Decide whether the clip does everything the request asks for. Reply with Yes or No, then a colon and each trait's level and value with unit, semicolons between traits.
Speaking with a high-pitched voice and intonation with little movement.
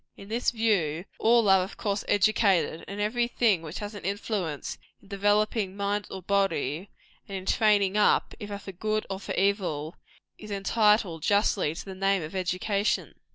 Yes: high, 200 Hz; narrow, 2.0 semitones